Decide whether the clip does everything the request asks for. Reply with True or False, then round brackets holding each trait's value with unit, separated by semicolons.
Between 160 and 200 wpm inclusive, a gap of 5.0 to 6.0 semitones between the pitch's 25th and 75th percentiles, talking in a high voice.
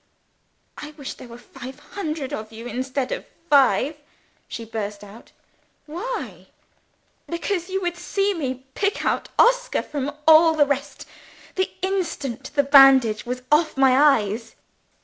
False (140 wpm; 5.4 semitones; 280 Hz)